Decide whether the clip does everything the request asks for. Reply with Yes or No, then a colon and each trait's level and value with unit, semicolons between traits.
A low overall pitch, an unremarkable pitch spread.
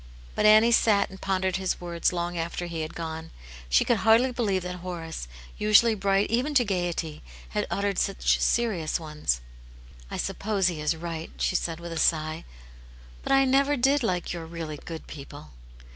No: medium, 180 Hz; average, 4.7 semitones